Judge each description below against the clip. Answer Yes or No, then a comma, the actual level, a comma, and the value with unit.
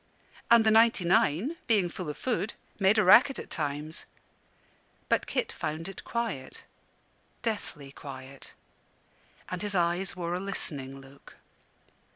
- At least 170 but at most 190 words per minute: No, slow, 135 wpm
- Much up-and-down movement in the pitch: Yes, wide, 6.5 semitones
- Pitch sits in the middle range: Yes, medium, 180 Hz